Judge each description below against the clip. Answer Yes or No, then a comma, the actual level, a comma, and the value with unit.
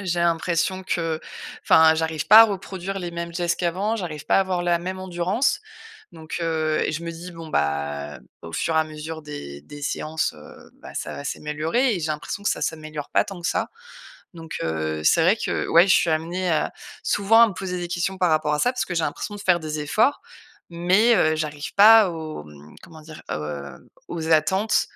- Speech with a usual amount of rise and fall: Yes, average, 3.2 semitones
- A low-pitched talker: No, medium, 165 Hz